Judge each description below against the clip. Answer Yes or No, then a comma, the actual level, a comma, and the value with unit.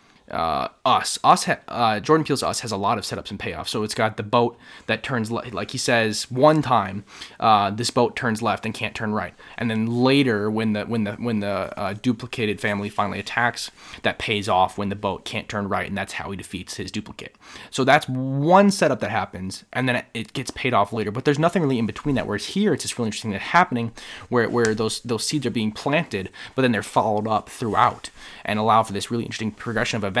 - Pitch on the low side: Yes, low, 115 Hz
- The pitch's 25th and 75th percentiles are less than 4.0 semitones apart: Yes, average, 3.2 semitones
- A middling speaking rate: No, fast, 235 wpm